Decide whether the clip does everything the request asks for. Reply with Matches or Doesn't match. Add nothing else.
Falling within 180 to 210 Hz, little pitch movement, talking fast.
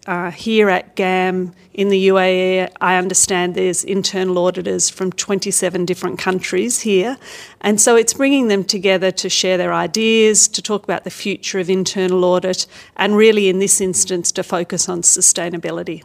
Matches